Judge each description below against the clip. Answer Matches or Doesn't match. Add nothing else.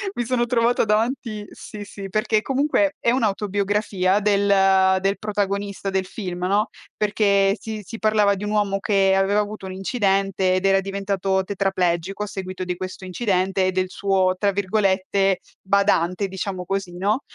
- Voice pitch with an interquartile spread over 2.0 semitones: Doesn't match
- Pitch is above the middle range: Matches